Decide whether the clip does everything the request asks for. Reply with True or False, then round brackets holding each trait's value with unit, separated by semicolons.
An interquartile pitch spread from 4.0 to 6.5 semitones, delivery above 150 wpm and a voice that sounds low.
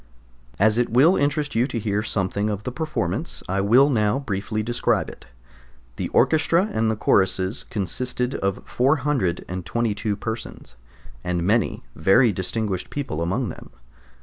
False (4.6 semitones; 135 wpm; 110 Hz)